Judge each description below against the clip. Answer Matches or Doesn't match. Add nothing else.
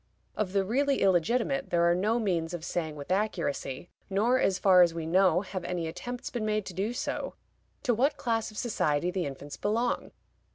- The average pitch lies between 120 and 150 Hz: Doesn't match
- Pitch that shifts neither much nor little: Matches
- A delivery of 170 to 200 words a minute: Matches